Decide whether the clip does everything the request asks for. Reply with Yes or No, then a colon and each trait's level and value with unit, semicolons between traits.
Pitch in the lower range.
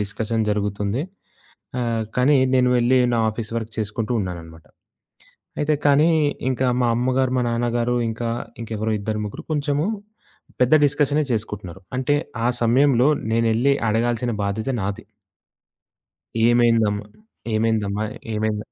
Yes: low, 115 Hz